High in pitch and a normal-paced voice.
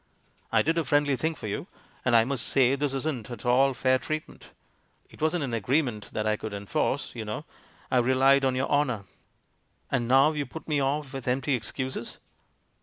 No: low, 130 Hz; average, 195 wpm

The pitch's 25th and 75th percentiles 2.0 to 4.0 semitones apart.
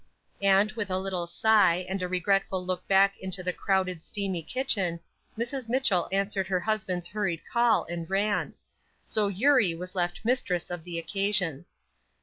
Yes: average, 2.8 semitones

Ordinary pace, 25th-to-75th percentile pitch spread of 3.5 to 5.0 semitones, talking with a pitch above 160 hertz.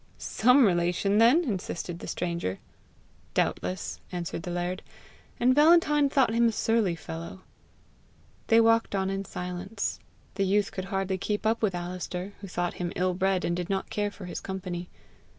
Yes: average, 165 wpm; average, 3.9 semitones; high, 190 Hz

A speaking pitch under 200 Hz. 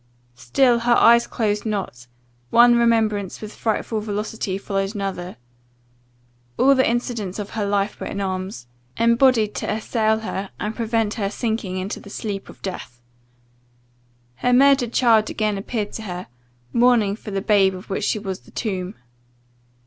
No: high, 210 Hz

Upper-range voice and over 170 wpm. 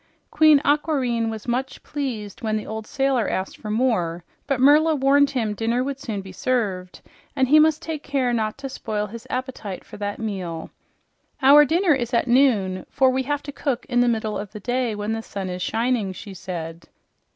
Yes: high, 235 Hz; average, 195 wpm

